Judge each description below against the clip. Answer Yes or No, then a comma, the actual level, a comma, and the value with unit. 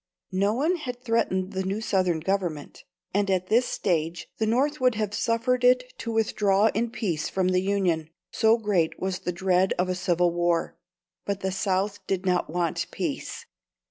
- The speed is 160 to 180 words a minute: Yes, average, 175 wpm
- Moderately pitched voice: No, high, 195 Hz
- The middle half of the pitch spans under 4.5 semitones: Yes, average, 3.7 semitones